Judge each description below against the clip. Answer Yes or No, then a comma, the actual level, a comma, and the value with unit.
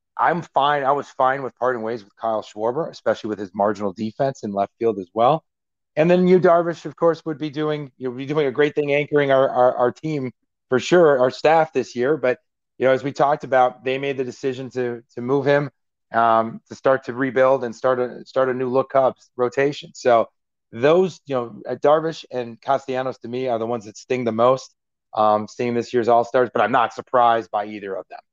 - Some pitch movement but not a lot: Yes, average, 3.1 semitones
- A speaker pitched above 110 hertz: Yes, low, 130 Hz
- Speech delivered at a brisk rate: Yes, fast, 225 wpm